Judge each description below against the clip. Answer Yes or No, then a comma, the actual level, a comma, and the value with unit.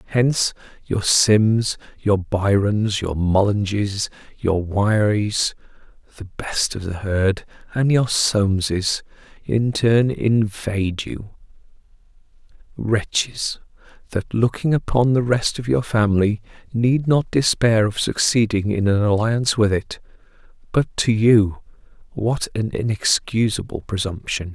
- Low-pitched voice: Yes, low, 105 Hz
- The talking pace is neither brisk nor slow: No, slow, 110 wpm